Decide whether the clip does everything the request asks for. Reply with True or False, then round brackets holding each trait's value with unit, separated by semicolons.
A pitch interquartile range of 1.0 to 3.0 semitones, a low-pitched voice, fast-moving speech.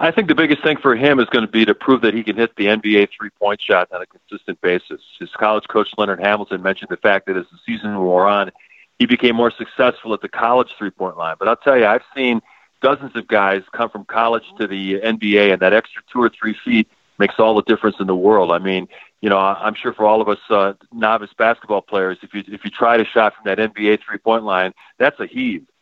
True (2.5 semitones; 110 Hz; 245 wpm)